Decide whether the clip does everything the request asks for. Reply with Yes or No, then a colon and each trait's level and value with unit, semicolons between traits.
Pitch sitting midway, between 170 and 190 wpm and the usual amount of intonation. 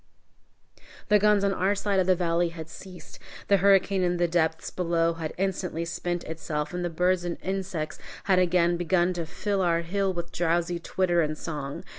No: medium, 175 Hz; average, 185 wpm; narrow, 2.1 semitones